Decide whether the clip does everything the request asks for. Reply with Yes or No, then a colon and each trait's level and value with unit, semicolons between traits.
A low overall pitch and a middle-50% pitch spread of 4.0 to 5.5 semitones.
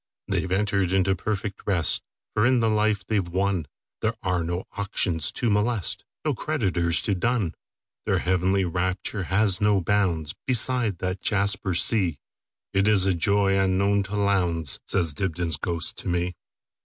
No: very low, 95 Hz; average, 2.7 semitones